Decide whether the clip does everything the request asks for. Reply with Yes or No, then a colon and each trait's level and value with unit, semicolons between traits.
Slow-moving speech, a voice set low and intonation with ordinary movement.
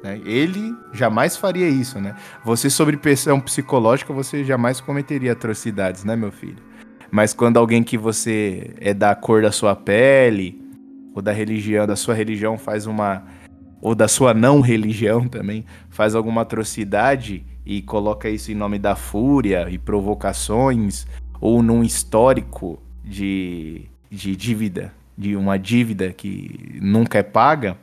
No: average, 140 wpm; low, 110 Hz; average, 3.3 semitones